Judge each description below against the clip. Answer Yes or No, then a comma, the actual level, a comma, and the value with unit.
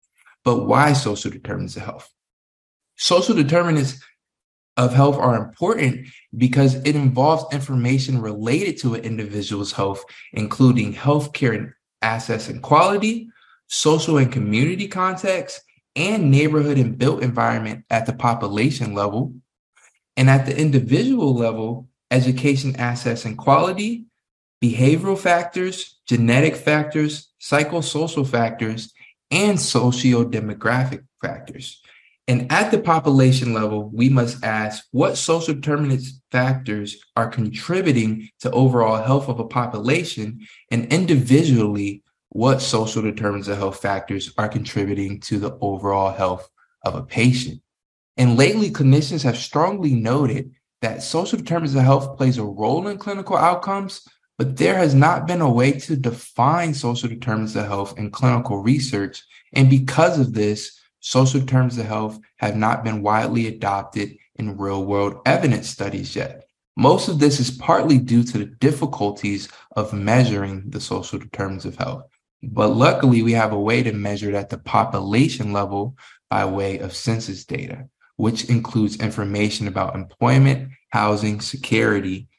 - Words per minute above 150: No, slow, 135 wpm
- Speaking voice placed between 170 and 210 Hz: No, low, 125 Hz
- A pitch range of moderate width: Yes, average, 4.5 semitones